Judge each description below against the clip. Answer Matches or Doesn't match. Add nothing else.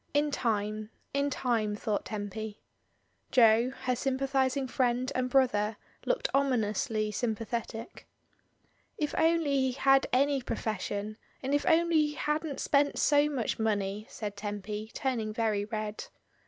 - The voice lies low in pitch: Doesn't match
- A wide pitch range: Doesn't match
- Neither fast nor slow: Doesn't match